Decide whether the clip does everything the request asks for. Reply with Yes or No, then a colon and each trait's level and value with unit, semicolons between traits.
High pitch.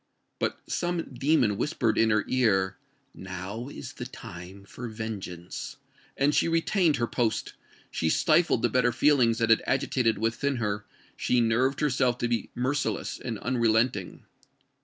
No: low, 120 Hz